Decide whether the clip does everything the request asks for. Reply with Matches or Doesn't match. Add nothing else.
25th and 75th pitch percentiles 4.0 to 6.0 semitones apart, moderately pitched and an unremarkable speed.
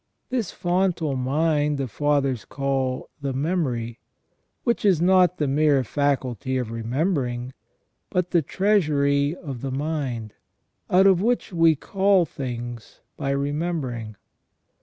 Doesn't match